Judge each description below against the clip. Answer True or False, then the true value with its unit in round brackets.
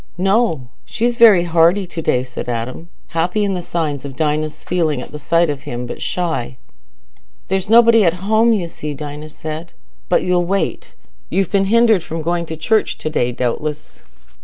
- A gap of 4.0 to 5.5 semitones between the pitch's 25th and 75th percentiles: True (4.5 semitones)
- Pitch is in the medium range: True (170 Hz)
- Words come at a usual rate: True (180 wpm)